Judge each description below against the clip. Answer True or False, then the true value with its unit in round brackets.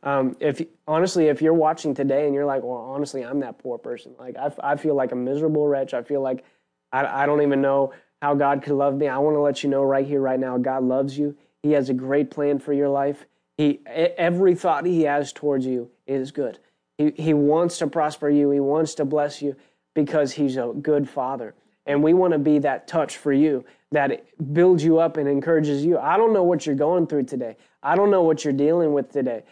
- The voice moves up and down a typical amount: False (2.0 semitones)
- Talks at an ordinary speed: False (235 wpm)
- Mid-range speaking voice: True (145 Hz)